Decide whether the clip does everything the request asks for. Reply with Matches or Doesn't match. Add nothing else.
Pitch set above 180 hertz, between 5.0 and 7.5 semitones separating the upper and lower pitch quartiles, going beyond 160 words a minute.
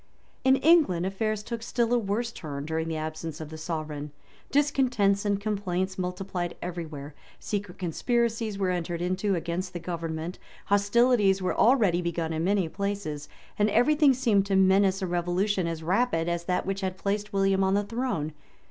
Doesn't match